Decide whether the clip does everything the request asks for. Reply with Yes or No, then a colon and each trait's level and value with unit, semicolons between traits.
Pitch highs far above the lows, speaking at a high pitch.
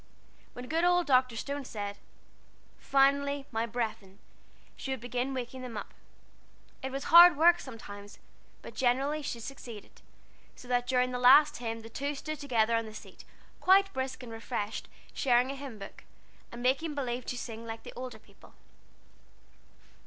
No: average, 3.5 semitones; very high, 250 Hz